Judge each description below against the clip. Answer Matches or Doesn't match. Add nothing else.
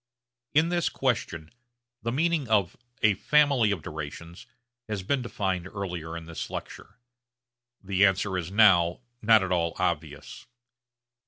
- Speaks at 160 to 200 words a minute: Doesn't match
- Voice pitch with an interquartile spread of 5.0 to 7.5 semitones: Matches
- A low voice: Matches